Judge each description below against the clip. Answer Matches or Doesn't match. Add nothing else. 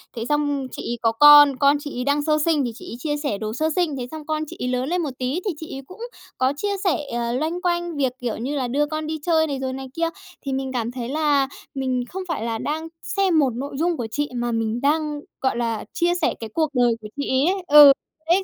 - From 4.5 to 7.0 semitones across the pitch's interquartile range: Doesn't match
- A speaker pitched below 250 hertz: Doesn't match